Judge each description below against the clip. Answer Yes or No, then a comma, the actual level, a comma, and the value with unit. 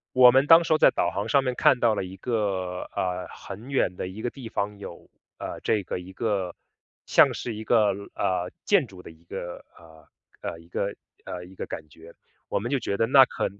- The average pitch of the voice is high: No, low, 100 Hz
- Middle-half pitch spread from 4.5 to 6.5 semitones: Yes, average, 5.1 semitones